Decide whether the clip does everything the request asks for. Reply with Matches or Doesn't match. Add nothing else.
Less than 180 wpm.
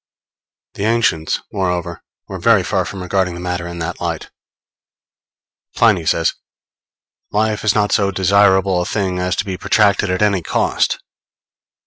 Matches